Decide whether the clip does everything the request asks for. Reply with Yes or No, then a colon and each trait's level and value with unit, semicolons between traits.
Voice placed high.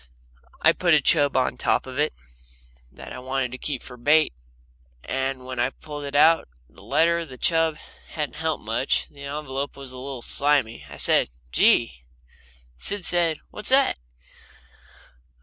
No: medium, 140 Hz